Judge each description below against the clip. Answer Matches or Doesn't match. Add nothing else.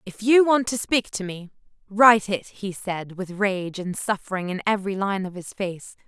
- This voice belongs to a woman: Matches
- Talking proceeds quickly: Matches